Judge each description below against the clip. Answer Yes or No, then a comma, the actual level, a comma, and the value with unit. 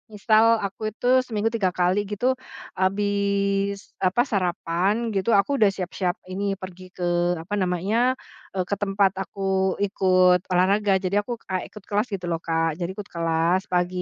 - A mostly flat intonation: Yes, narrow, 2.1 semitones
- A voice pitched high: Yes, high, 195 Hz